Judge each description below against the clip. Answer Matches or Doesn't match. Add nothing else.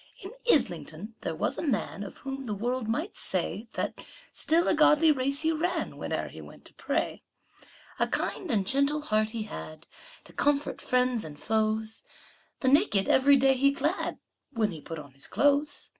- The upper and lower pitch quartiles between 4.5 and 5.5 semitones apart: Matches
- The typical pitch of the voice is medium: Doesn't match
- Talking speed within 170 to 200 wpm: Matches